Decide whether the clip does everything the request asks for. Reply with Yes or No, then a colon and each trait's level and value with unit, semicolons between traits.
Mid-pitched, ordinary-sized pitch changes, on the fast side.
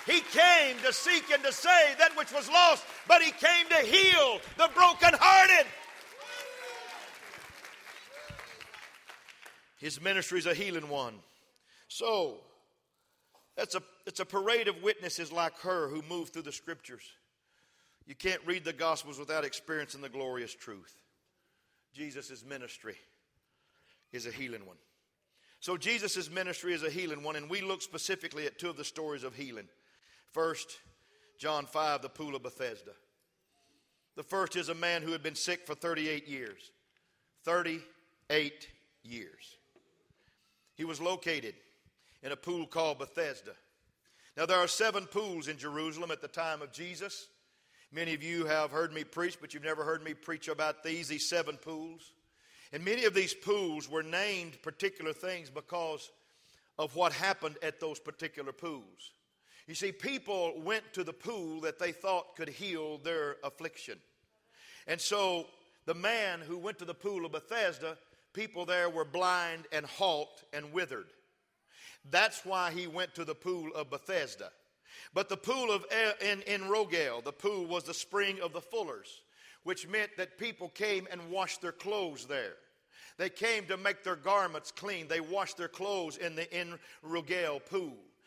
No: medium, 175 Hz; average, 4.2 semitones; average, 160 wpm